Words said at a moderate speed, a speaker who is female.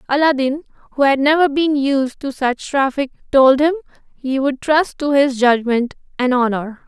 Yes: average, 165 wpm; female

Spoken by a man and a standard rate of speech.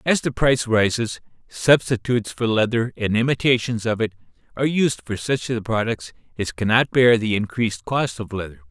Yes: male; average, 180 wpm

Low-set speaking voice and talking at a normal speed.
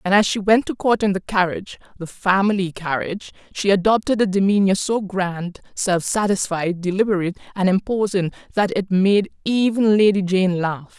No: high, 195 Hz; average, 165 wpm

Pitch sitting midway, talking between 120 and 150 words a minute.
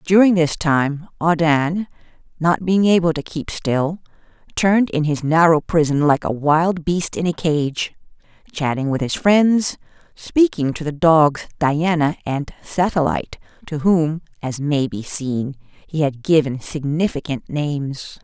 Yes: medium, 160 Hz; average, 145 wpm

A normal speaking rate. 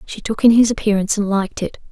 No: fast, 250 wpm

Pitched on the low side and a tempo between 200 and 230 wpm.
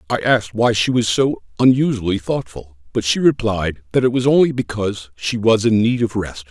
Yes: low, 110 Hz; fast, 205 wpm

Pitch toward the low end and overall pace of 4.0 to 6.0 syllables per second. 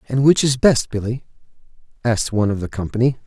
No: low, 120 Hz; 6.7 syllables/s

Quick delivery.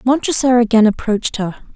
No: slow, 135 wpm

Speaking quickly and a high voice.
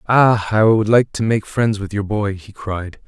No: fast, 255 wpm; low, 105 Hz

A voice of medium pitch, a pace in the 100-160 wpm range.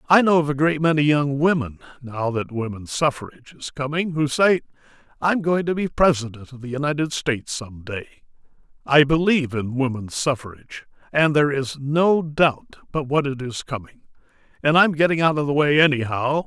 No: medium, 145 Hz; average, 190 wpm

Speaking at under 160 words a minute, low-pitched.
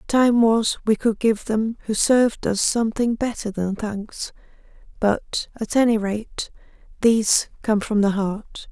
No: average, 150 wpm; high, 220 Hz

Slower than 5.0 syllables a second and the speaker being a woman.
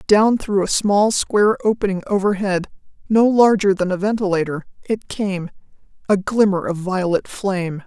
Yes: 4.8 syllables/s; female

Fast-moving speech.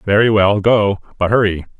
No: average, 165 wpm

